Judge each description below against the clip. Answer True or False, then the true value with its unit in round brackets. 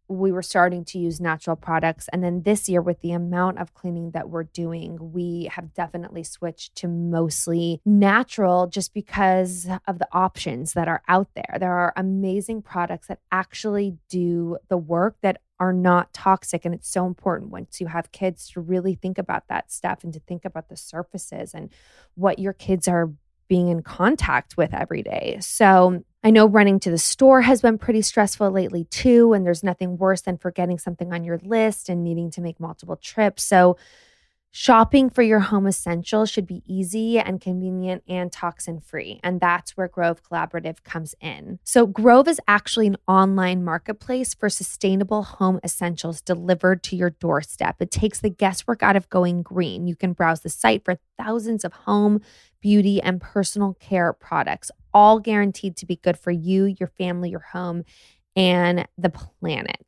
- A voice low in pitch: False (185 Hz)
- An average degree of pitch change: False (2.3 semitones)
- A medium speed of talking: True (180 wpm)